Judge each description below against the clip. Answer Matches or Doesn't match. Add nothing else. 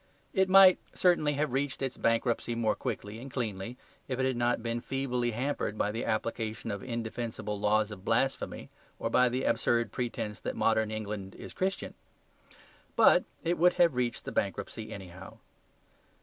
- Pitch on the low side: Matches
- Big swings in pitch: Doesn't match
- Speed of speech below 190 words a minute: Matches